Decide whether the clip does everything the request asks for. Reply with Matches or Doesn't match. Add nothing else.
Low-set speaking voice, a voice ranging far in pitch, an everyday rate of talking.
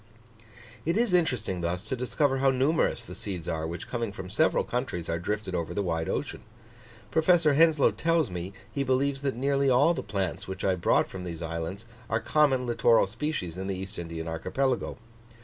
Matches